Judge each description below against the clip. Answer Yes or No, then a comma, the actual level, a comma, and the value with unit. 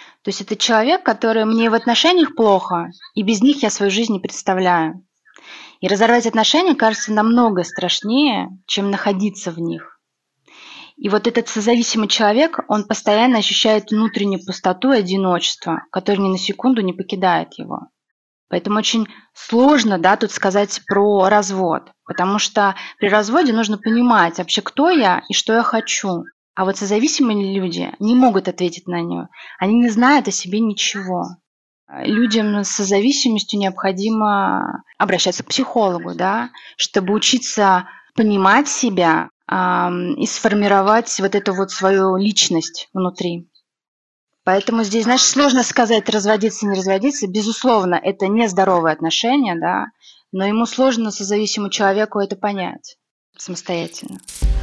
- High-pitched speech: Yes, high, 210 Hz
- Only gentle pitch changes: No, average, 3.2 semitones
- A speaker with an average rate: Yes, average, 135 wpm